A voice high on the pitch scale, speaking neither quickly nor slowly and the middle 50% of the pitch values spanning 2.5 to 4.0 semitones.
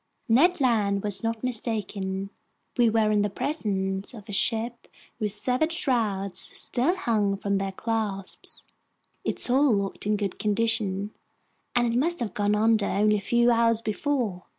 Yes: high, 215 Hz; average, 155 wpm; average, 3.1 semitones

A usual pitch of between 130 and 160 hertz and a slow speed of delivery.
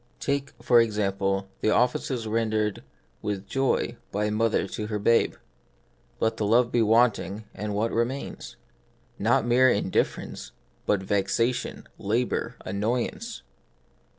No: low, 110 Hz; slow, 125 wpm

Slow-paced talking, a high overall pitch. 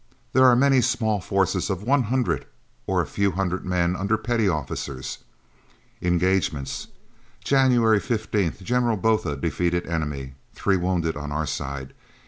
No: slow, 130 wpm; very low, 95 Hz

